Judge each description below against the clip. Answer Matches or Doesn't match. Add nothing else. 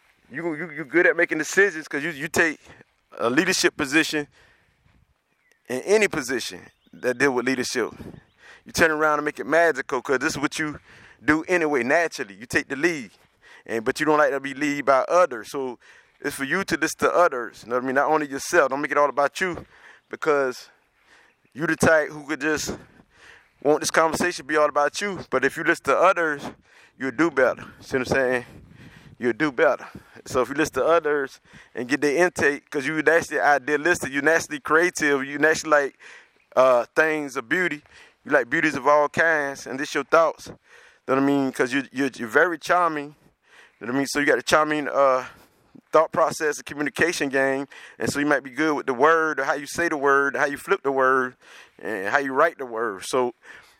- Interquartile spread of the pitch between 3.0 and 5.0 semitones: Doesn't match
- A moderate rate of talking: Doesn't match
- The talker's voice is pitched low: Doesn't match